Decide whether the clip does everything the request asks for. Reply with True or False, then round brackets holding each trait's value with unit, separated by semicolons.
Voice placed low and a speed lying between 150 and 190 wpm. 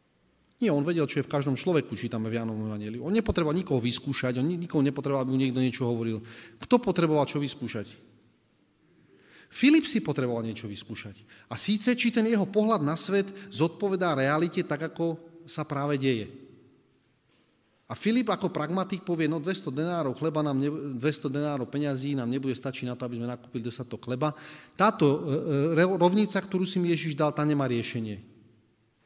False (145 Hz; 165 wpm)